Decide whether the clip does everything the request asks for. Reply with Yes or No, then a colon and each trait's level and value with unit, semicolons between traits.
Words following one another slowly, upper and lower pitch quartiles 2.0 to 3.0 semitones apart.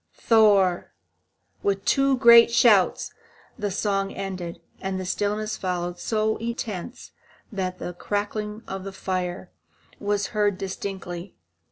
Yes: slow, 120 wpm; narrow, 2.5 semitones